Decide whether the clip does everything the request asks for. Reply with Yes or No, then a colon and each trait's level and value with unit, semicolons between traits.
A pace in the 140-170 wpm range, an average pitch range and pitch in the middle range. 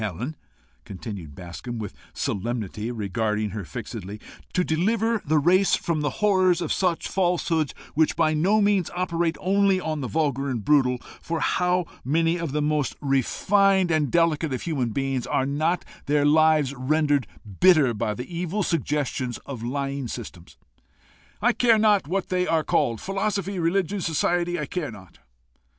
No: average, 160 wpm; wide, 6.1 semitones; medium, 155 Hz